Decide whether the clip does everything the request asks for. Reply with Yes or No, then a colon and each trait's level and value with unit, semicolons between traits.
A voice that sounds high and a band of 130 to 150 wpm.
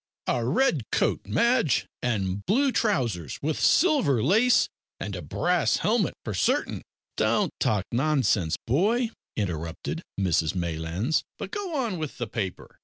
No: low, 130 Hz; average, 140 wpm